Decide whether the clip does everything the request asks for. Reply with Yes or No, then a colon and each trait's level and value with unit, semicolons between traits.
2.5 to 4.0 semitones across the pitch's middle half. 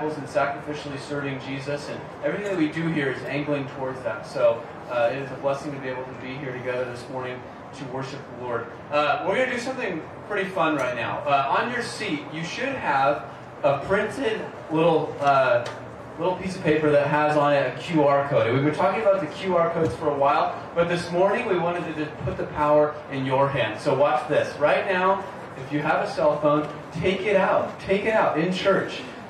Yes: average, 3.6 semitones